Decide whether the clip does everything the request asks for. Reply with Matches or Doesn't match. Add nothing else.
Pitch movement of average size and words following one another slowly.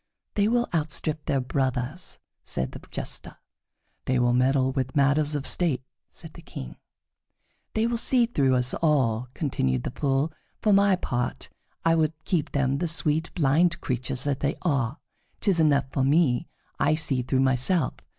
Doesn't match